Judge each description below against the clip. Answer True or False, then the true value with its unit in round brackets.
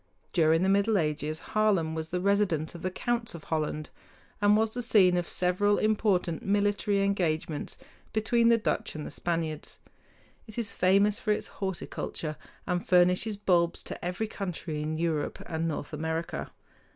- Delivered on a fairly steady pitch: False (4.2 semitones)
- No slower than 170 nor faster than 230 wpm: False (160 wpm)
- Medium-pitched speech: True (180 Hz)